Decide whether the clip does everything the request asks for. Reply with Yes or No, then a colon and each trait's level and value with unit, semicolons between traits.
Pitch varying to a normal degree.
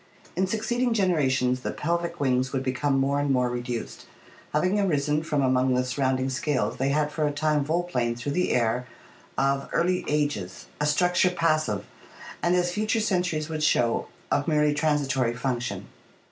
Yes: average, 4.6 semitones